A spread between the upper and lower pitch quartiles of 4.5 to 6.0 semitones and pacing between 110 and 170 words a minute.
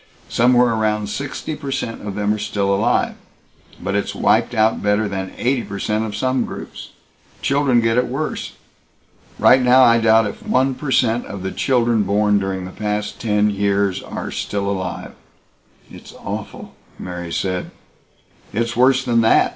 No: average, 3.4 semitones; average, 165 wpm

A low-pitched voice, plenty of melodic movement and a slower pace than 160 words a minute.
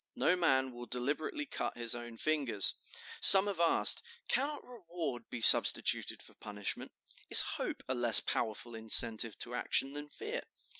Yes: low, 130 Hz; wide, 6.5 semitones; average, 150 wpm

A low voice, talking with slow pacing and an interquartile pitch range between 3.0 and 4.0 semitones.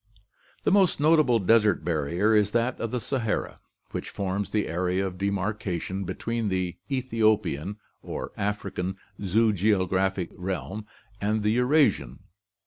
Yes: low, 105 Hz; slow, 125 wpm; average, 3.4 semitones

